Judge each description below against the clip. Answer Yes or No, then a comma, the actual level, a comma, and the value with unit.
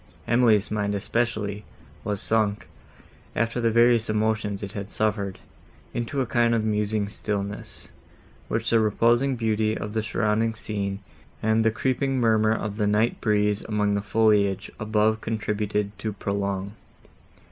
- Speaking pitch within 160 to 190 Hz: No, low, 110 Hz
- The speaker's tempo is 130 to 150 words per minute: Yes, average, 140 wpm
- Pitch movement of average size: No, narrow, 1.6 semitones